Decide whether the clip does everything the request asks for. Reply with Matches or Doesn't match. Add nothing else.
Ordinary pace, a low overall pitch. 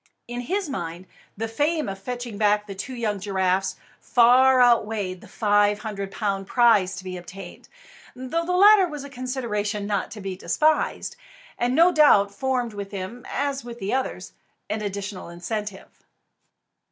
Doesn't match